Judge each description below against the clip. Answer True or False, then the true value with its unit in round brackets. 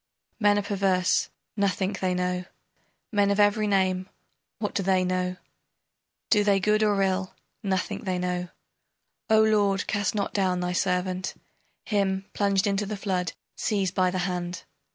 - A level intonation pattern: True (1.9 semitones)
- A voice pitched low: False (195 Hz)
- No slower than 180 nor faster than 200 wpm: False (155 wpm)